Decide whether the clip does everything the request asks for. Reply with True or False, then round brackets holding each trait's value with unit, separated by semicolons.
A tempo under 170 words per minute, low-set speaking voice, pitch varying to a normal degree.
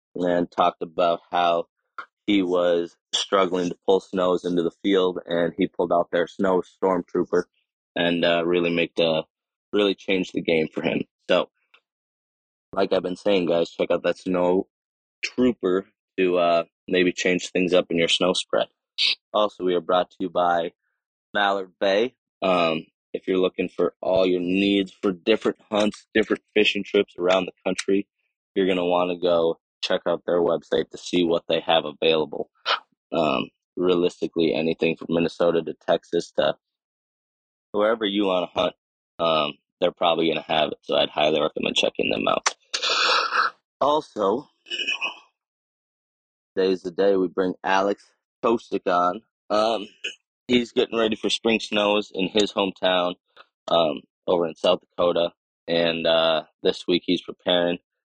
False (155 wpm; 90 Hz; 2.1 semitones)